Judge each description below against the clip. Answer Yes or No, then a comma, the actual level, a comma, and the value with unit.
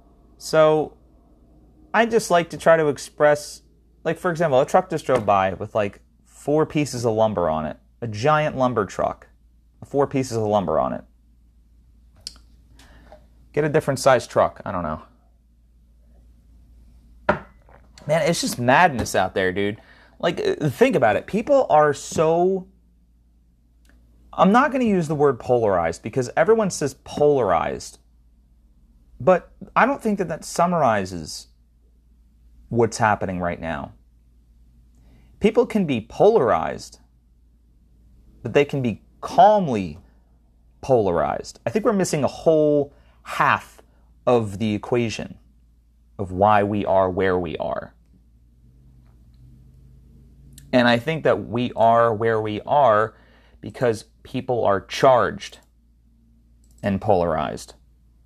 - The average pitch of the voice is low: Yes, very low, 90 Hz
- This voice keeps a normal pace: No, slow, 125 wpm